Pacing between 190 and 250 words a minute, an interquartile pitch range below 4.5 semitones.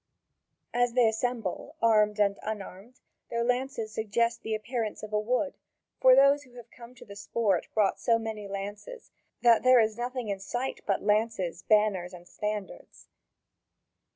No: average, 155 wpm; average, 2.8 semitones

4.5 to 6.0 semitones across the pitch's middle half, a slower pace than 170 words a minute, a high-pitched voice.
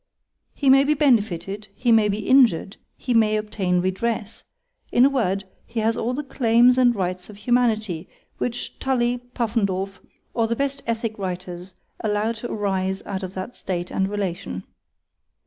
No: average, 3.9 semitones; average, 150 wpm; high, 215 Hz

